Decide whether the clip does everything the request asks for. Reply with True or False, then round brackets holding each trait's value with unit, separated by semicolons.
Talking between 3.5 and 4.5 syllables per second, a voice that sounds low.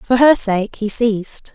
False (4.0 syllables/s; 225 Hz)